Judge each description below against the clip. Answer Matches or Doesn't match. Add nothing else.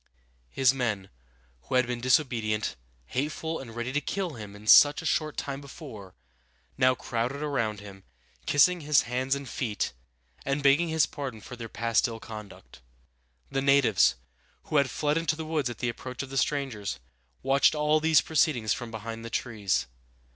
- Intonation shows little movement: Doesn't match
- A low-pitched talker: Matches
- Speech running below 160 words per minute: Doesn't match